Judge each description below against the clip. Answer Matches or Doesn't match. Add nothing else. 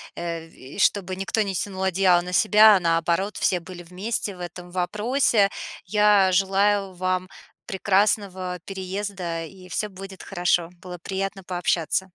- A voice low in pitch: Doesn't match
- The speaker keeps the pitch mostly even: Matches